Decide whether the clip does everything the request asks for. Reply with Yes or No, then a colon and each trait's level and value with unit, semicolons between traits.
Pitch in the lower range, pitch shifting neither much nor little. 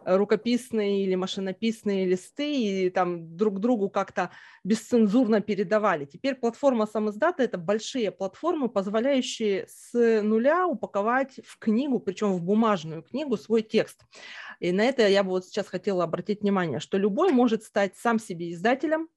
No: high, 215 Hz; average, 3.4 semitones